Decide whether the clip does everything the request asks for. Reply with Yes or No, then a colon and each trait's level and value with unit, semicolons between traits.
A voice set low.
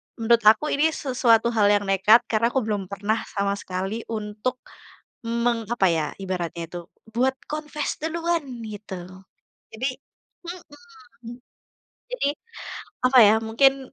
No: high, 230 Hz